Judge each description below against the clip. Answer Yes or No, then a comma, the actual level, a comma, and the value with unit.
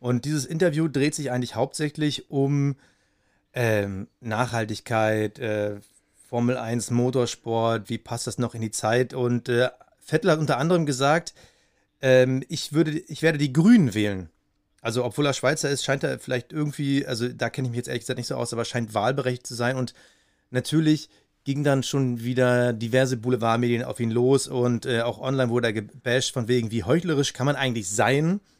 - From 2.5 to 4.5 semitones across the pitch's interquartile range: Yes, average, 3.3 semitones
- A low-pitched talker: Yes, low, 125 Hz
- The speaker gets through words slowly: No, average, 185 wpm